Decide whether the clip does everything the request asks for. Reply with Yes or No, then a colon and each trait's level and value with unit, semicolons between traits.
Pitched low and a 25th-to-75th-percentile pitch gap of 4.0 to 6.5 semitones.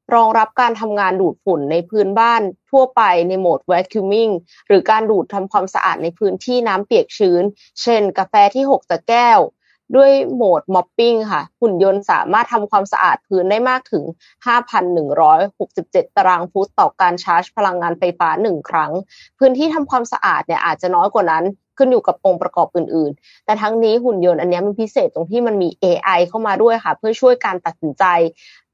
No: high, 200 Hz; average, 4.5 semitones